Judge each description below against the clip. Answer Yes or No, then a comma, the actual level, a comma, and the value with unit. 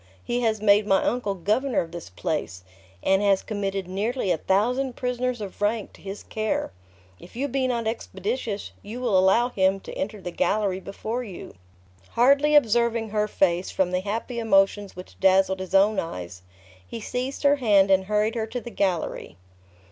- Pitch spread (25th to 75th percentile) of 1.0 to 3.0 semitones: No, average, 3.7 semitones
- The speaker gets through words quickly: No, average, 180 wpm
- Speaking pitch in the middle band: No, high, 210 Hz